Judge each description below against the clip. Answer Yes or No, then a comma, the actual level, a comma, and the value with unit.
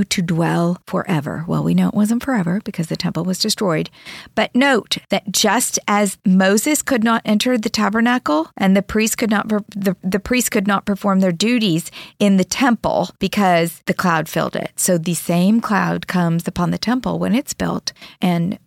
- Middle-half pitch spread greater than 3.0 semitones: Yes, average, 3.4 semitones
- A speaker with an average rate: Yes, average, 185 wpm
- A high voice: Yes, high, 195 Hz